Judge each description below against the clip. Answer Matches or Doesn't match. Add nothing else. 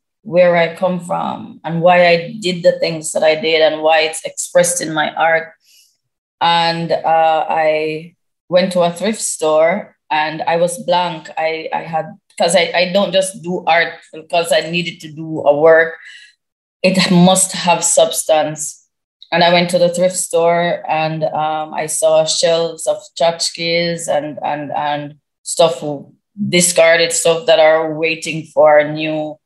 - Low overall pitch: Doesn't match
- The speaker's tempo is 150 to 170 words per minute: Matches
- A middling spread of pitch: Doesn't match